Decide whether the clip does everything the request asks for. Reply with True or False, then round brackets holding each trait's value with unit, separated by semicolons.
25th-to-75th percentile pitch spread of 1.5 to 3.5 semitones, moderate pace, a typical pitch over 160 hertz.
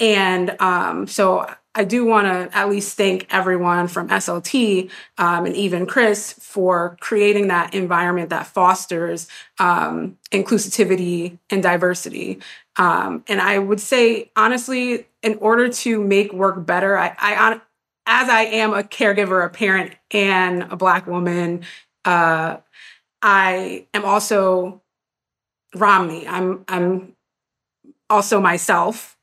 False (2.8 semitones; 125 wpm; 190 Hz)